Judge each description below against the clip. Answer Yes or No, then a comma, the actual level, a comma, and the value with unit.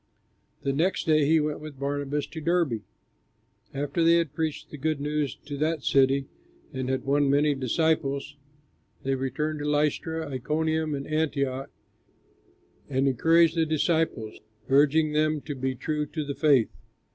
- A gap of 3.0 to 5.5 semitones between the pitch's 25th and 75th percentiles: No, narrow, 2.4 semitones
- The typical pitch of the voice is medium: Yes, medium, 150 Hz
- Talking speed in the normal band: Yes, average, 150 wpm